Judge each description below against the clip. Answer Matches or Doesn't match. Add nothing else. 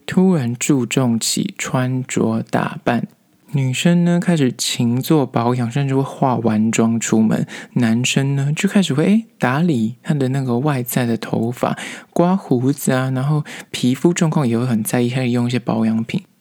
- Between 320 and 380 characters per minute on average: Doesn't match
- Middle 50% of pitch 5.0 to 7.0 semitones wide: Matches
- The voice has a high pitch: Doesn't match